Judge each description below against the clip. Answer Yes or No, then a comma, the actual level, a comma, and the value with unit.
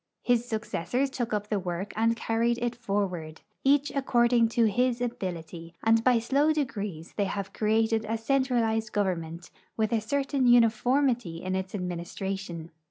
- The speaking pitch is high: Yes, high, 225 Hz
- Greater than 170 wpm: No, average, 150 wpm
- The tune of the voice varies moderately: Yes, average, 4.1 semitones